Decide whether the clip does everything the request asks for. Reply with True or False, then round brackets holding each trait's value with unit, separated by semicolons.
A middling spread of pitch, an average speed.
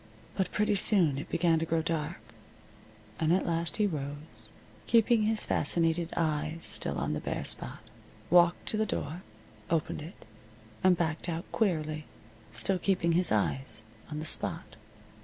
True (3.2 semitones; 155 wpm)